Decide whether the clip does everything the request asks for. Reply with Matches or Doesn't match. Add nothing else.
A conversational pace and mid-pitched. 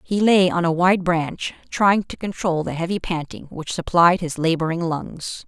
Matches